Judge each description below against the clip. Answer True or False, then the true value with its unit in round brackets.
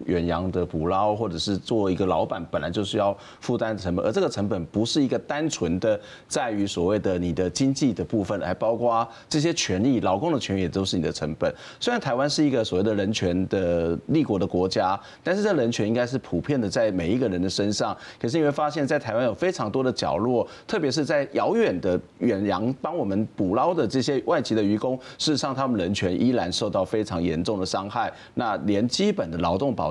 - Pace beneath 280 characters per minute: False (335 characters per minute)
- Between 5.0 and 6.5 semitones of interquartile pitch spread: True (5.5 semitones)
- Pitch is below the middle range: True (105 Hz)